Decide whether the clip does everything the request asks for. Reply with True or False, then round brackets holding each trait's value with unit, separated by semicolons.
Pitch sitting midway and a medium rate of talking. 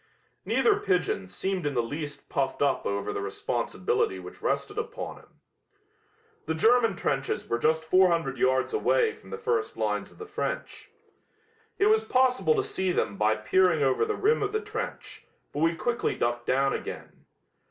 True (170 Hz; 170 wpm)